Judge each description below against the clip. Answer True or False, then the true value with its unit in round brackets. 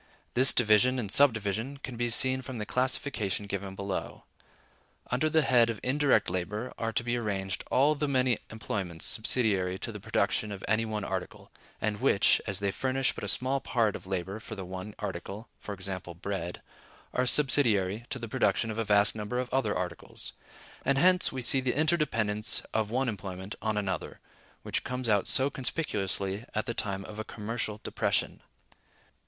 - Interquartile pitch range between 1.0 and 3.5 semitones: False (4.4 semitones)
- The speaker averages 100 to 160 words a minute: False (175 wpm)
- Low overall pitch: True (110 Hz)